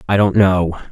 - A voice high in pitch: No, very low, 95 Hz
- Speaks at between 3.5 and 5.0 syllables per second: Yes, 4.6 syllables/s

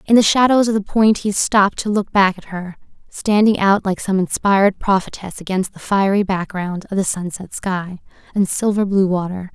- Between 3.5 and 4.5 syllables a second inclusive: No, 5.0 syllables/s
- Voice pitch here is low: No, high, 195 Hz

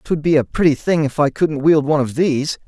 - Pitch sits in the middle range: Yes, medium, 150 Hz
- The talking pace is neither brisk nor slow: No, fast, 270 wpm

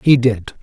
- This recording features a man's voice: Yes, male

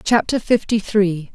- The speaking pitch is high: Yes, high, 200 Hz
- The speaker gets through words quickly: No, slow, 135 wpm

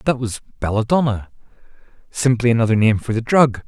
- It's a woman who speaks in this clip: No, male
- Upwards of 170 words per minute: No, average, 145 wpm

